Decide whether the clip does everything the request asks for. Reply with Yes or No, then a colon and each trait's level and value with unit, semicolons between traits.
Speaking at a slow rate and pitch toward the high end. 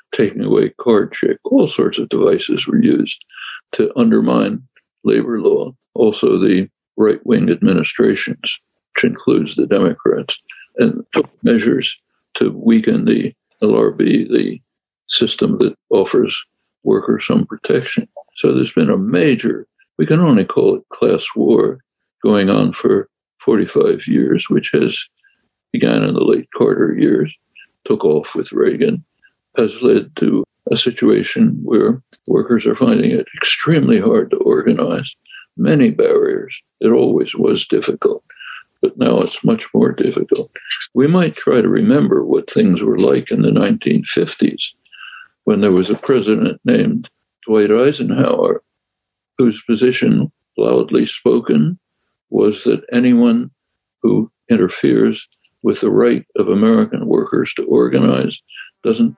Yes: slow, 130 wpm; very high, 390 Hz